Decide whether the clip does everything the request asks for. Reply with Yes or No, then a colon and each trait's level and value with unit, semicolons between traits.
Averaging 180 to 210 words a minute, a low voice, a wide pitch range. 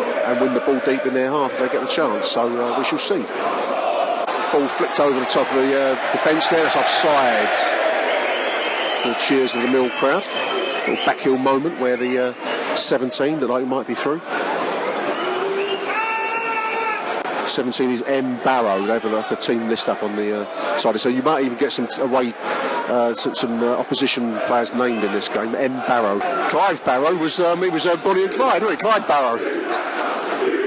Yes: average, 195 wpm; low, 130 Hz; wide, 7.9 semitones